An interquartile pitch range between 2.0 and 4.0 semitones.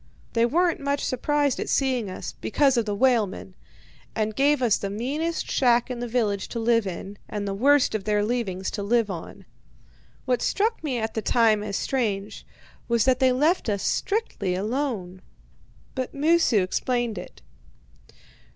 No: average, 4.5 semitones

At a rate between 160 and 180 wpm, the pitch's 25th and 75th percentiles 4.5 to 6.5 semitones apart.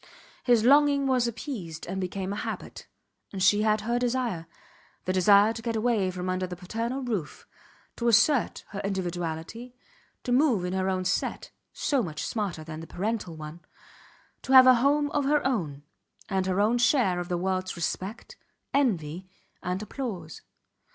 Yes: average, 165 wpm; average, 5.2 semitones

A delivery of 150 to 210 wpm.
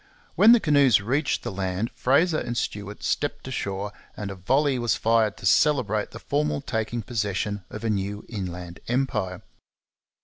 Yes: average, 160 wpm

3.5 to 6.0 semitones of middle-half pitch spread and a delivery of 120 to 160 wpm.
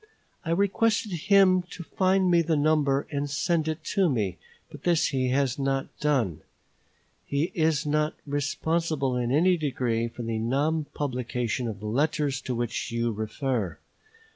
Yes: average, 4.7 semitones; average, 155 wpm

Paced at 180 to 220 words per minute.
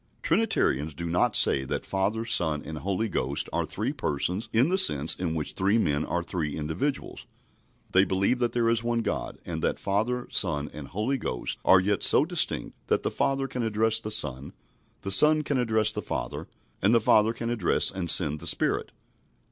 Yes: average, 195 wpm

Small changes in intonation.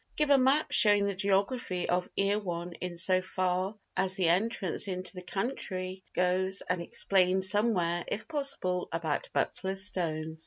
Yes: narrow, 2.0 semitones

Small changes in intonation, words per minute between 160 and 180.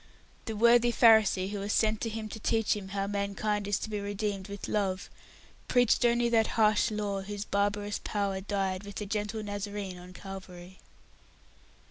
Yes: narrow, 1.6 semitones; average, 170 wpm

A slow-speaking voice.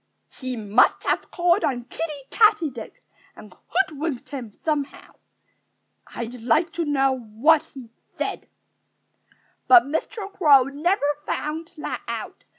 Yes: slow, 120 wpm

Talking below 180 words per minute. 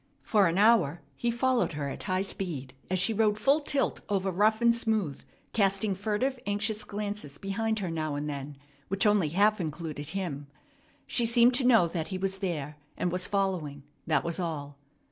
No: average, 185 wpm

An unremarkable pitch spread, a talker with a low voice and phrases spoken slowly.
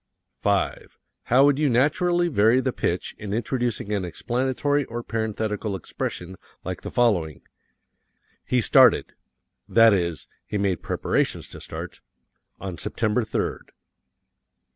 Yes: average, 4.4 semitones; low, 115 Hz; slow, 120 wpm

